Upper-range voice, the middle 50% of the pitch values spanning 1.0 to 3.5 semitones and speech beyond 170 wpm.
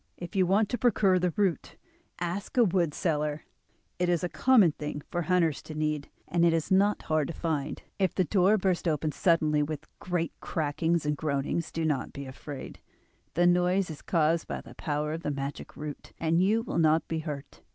No: medium, 165 Hz; average, 3.1 semitones; average, 200 wpm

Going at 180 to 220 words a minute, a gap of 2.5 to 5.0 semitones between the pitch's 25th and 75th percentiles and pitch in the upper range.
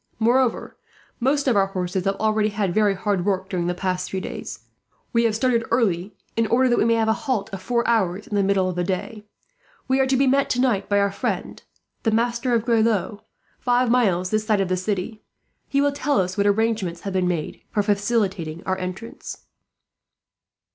Yes: average, 200 wpm; average, 3.8 semitones; high, 210 Hz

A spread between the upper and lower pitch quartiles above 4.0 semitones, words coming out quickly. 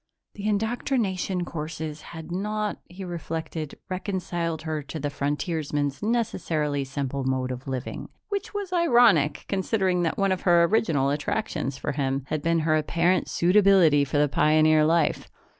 No: average, 4.6 semitones; average, 145 wpm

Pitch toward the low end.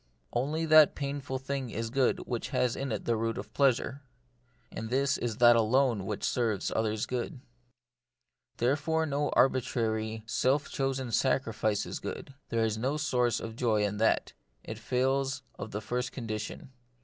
Yes: low, 125 Hz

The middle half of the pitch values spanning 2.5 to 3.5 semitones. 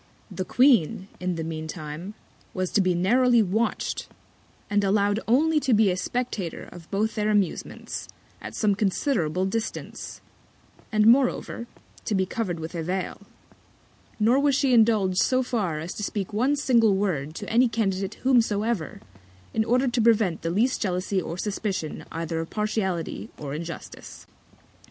No: average, 4.3 semitones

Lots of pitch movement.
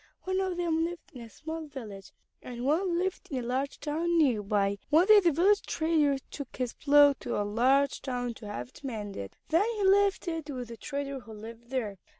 Yes: wide, 6.1 semitones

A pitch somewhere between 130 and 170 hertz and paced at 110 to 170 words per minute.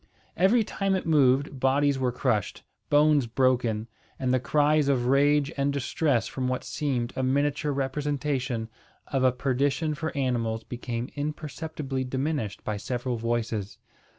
Yes: low, 135 Hz; average, 140 wpm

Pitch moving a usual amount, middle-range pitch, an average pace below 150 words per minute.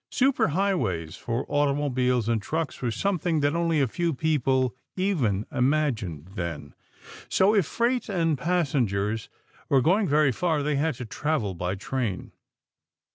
No: wide, 6.3 semitones; medium, 145 Hz; average, 140 wpm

